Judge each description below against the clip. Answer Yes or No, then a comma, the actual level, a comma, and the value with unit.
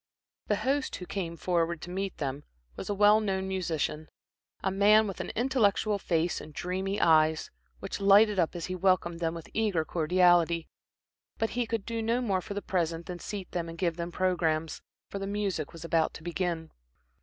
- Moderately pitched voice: Yes, medium, 180 Hz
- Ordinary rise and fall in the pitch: Yes, average, 3.3 semitones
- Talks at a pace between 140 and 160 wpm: No, average, 190 wpm